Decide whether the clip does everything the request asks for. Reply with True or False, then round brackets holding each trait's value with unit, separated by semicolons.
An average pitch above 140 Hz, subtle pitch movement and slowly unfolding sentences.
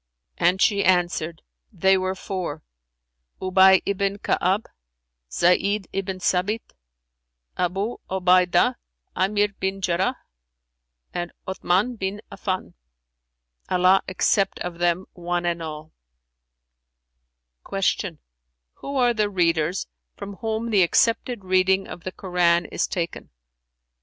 True (185 Hz; 2.2 semitones; 105 wpm)